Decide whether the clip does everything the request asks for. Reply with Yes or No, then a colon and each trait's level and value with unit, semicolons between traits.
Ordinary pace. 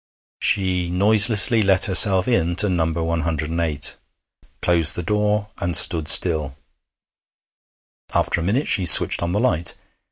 No: slow, 125 wpm